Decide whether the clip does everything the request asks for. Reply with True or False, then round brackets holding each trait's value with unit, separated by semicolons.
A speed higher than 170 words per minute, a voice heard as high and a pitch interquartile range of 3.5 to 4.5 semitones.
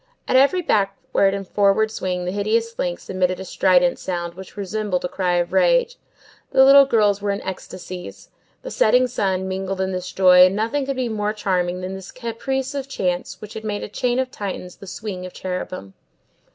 True (200 wpm; 195 Hz; 4.0 semitones)